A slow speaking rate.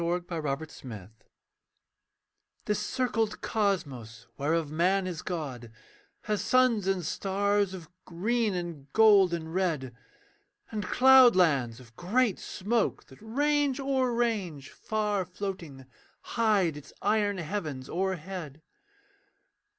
Yes: slow, 110 wpm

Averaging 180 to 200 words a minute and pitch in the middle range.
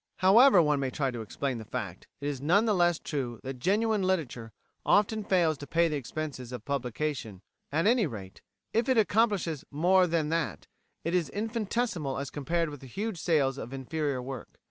Yes: average, 190 wpm; medium, 155 Hz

